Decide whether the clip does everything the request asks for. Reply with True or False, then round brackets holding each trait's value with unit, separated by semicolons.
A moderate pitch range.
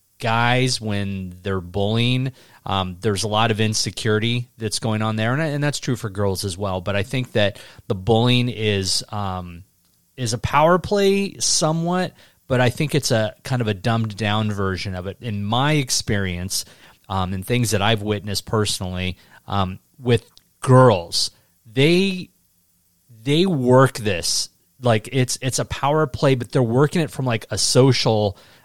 True (4.3 semitones)